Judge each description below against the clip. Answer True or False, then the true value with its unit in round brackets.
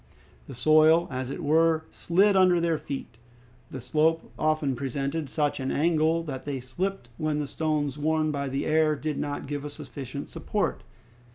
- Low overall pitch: False (150 Hz)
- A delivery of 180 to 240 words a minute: False (170 wpm)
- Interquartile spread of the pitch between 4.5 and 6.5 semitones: False (2.4 semitones)